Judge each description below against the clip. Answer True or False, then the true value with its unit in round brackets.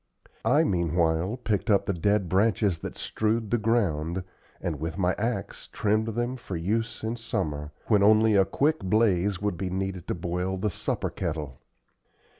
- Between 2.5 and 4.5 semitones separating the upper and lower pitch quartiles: True (4.2 semitones)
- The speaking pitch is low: True (100 Hz)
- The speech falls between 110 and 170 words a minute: True (165 wpm)